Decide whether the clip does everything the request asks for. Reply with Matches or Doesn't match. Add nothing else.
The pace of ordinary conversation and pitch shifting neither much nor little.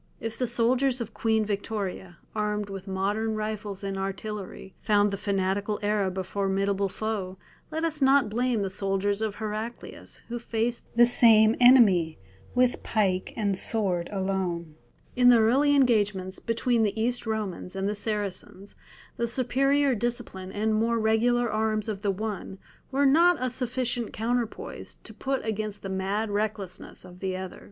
Matches